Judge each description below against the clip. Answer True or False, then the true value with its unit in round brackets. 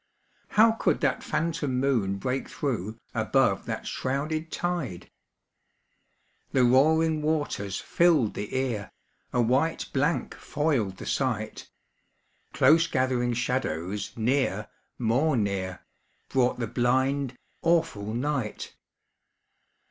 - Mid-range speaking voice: False (130 Hz)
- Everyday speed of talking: False (105 wpm)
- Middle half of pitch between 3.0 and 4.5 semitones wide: False (5.4 semitones)